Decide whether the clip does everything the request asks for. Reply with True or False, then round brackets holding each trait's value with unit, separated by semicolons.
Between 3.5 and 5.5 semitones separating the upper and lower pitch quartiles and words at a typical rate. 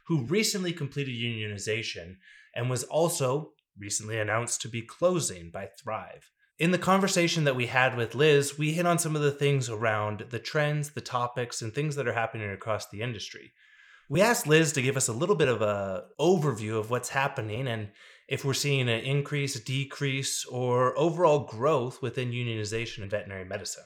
True (4.6 semitones; 180 wpm)